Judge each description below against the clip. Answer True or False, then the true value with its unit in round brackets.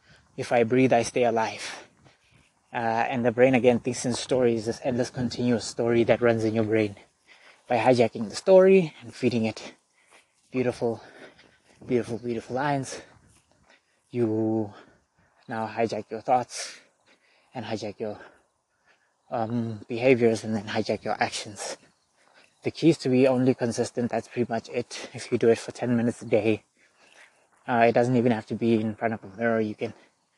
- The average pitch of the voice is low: True (115 Hz)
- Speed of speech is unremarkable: True (165 wpm)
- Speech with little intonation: True (1.8 semitones)